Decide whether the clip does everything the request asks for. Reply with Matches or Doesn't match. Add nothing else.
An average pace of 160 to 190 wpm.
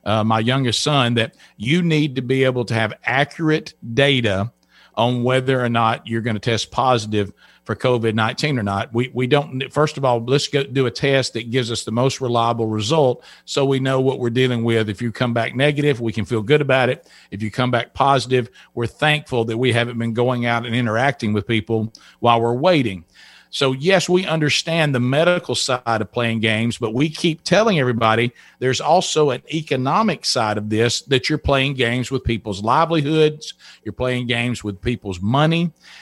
Doesn't match